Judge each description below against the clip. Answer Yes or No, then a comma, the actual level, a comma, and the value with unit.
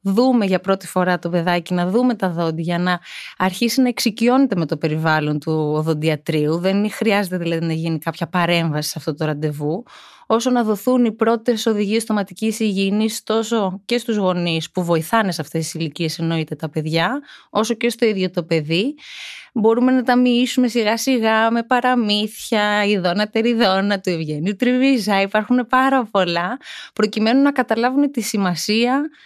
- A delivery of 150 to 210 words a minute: Yes, average, 160 wpm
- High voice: Yes, high, 205 Hz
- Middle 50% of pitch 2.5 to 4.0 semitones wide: No, wide, 5.6 semitones